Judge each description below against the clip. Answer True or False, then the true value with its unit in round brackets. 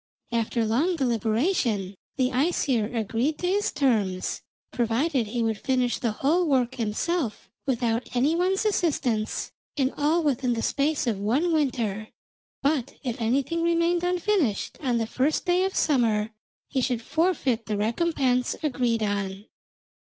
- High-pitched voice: True (255 Hz)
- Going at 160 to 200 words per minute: False (140 wpm)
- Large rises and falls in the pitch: True (5.8 semitones)